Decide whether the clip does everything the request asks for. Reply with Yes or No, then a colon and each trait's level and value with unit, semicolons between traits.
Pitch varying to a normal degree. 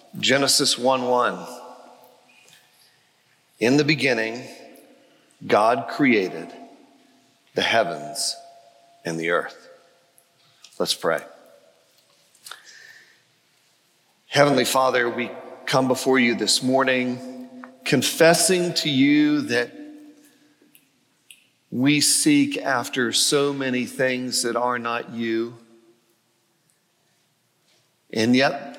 No: wide, 6.1 semitones